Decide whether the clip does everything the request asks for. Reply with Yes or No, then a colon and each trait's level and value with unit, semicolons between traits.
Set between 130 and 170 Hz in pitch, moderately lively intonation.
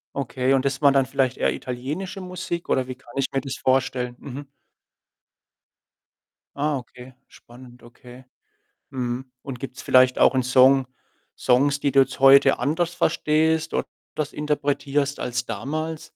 No: low, 135 Hz; narrow, 2.3 semitones